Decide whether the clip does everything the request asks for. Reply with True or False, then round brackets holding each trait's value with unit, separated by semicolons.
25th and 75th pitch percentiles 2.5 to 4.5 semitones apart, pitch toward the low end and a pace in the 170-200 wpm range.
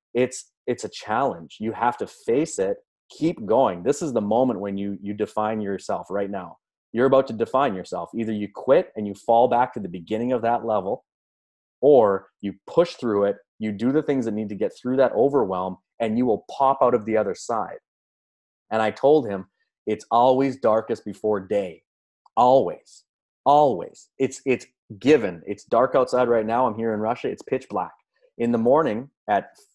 True (4.0 semitones; 110 Hz; 190 wpm)